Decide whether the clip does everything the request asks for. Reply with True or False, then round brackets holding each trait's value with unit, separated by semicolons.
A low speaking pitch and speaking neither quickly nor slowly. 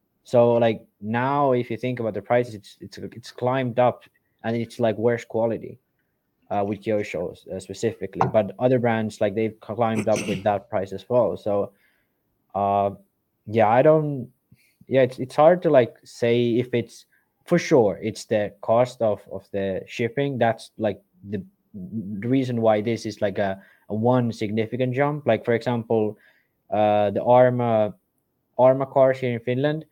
True (115 Hz; 170 wpm)